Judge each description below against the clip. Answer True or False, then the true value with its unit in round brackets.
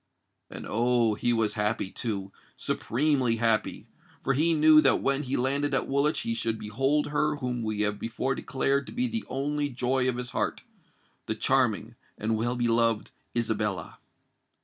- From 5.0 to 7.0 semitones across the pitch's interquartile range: False (3.7 semitones)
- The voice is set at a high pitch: False (125 Hz)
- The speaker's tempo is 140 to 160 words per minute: True (155 wpm)